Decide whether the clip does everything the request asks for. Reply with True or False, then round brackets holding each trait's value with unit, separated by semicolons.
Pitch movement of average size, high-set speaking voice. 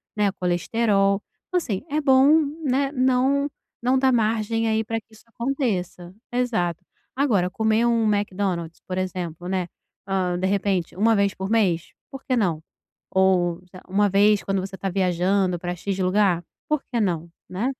True (4.2 semitones; 200 Hz)